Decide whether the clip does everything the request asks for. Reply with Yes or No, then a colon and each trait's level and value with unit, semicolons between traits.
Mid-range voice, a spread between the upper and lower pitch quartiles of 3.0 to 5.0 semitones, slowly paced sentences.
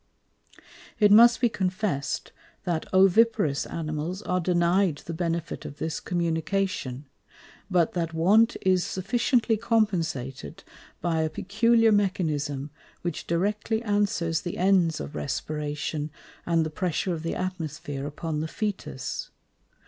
Yes: medium, 175 Hz; average, 4.2 semitones; slow, 120 wpm